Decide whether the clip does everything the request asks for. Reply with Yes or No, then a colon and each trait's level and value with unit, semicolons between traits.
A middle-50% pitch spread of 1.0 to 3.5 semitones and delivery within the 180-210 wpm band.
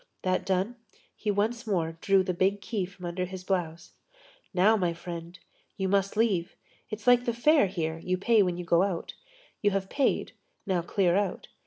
Yes: average, 2.7 semitones; average, 185 wpm